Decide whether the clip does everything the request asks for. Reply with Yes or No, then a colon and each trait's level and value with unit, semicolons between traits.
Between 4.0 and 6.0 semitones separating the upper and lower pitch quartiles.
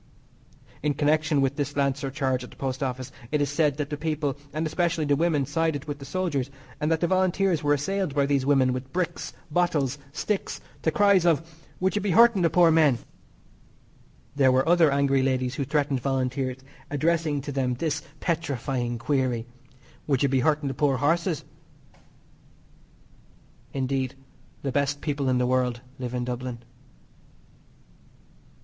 No: average, 3.4 semitones